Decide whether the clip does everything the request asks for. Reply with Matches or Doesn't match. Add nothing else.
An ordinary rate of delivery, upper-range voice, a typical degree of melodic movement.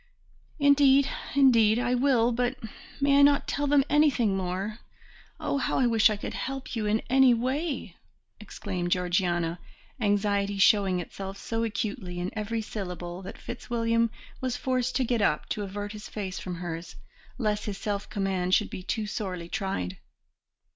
Matches